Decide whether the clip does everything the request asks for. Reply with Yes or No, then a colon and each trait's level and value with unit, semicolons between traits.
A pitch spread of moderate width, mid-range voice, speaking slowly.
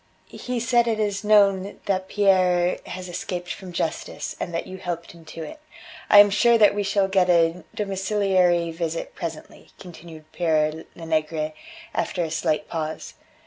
No: average, 3.3 semitones; medium, 180 Hz; average, 160 wpm